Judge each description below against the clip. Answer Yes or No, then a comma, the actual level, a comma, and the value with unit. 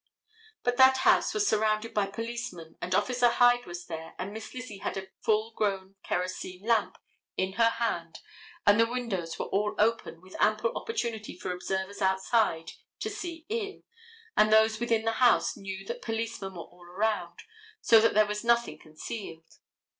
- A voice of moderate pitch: No, high, 215 Hz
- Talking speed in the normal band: Yes, average, 170 wpm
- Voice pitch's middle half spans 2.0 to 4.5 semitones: Yes, average, 3.6 semitones